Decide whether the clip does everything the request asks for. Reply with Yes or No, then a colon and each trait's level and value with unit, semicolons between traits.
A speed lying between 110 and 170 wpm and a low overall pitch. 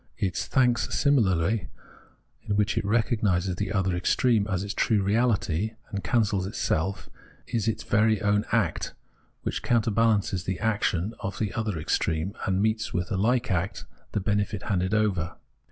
Yes: average, 155 wpm; low, 100 Hz